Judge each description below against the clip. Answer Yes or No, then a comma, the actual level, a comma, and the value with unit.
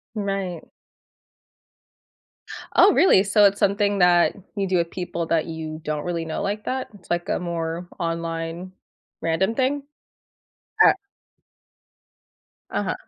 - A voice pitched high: No, medium, 180 Hz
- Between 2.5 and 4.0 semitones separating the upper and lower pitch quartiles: Yes, average, 3.3 semitones